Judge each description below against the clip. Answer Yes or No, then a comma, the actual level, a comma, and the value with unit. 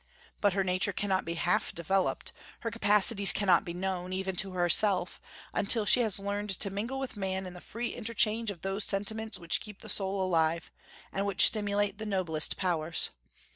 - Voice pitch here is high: Yes, high, 195 Hz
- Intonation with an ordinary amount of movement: No, narrow, 2.3 semitones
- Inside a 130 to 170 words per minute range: No, average, 180 wpm